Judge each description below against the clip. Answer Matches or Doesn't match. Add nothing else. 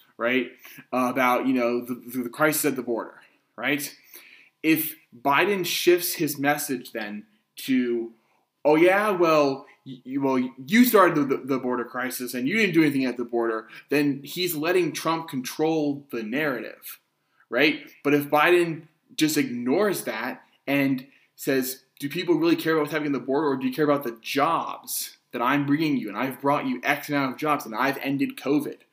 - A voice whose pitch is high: Doesn't match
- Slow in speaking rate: Doesn't match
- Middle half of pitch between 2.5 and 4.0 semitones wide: Matches